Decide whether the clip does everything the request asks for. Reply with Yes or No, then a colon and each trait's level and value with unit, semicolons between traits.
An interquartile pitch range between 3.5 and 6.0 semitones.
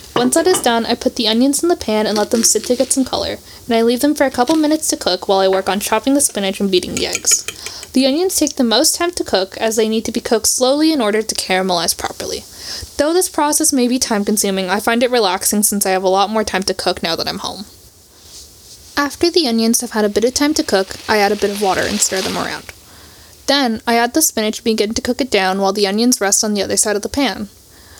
Yes: average, 5.3 semitones